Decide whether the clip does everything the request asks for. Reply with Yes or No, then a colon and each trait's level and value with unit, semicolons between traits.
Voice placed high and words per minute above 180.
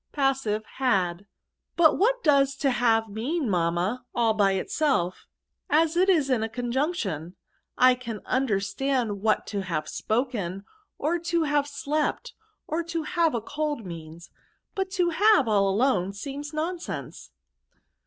No: very high, 255 Hz; average, 145 wpm